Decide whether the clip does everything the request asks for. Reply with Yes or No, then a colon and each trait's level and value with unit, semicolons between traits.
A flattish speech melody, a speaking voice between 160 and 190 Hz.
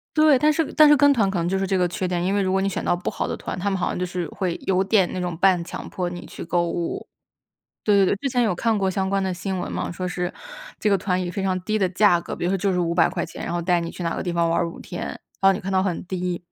Yes: narrow, 2.0 semitones; medium, 185 Hz